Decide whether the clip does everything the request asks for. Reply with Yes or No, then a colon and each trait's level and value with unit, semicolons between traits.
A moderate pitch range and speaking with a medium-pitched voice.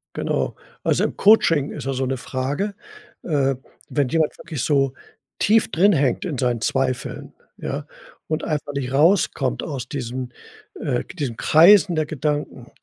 Yes: average, 3.7 semitones; medium, 145 Hz